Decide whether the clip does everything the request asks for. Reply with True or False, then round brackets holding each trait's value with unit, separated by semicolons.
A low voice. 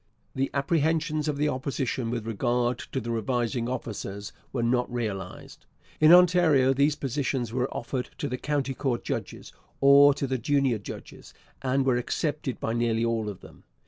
True (130 Hz)